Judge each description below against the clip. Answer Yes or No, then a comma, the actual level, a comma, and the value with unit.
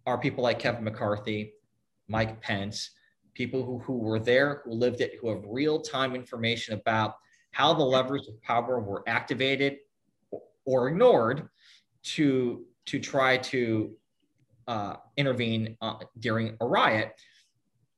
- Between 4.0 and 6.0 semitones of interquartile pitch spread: No, average, 3.0 semitones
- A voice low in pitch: Yes, low, 120 Hz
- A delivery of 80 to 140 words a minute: Yes, slow, 135 wpm